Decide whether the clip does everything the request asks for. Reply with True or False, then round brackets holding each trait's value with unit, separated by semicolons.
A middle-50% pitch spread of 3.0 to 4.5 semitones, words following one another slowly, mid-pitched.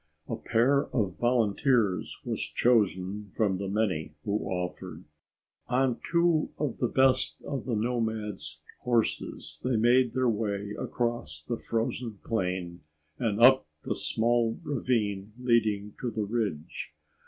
False (3.7 semitones; 130 wpm; 110 Hz)